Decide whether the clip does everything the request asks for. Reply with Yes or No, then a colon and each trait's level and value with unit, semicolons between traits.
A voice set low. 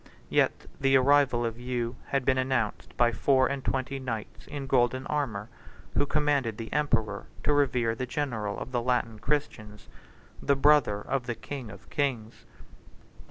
Yes: low, 130 Hz